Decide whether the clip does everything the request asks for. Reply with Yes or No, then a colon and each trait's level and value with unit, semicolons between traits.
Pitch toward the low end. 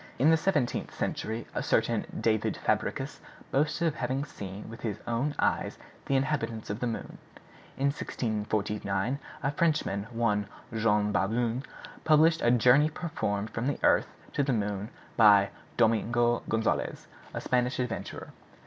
Yes: low, 120 Hz